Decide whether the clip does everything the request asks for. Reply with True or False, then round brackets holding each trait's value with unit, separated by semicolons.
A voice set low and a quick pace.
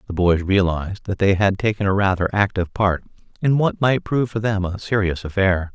True (100 Hz; 210 wpm)